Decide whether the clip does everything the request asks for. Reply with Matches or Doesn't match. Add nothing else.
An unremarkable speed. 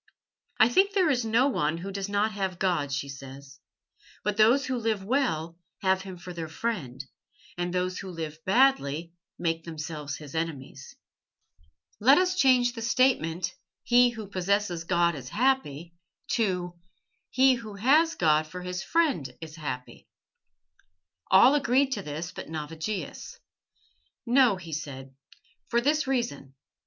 Matches